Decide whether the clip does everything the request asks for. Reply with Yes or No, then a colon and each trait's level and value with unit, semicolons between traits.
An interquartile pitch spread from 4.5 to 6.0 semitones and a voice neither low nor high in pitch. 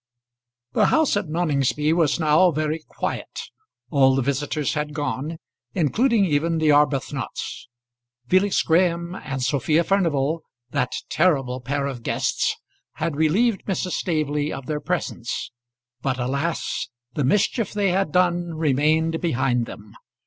No: average, 3.7 semitones; medium, 155 Hz